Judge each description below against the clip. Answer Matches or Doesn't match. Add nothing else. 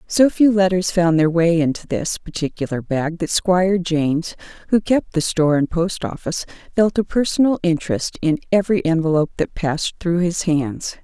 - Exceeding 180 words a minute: Doesn't match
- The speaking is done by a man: Doesn't match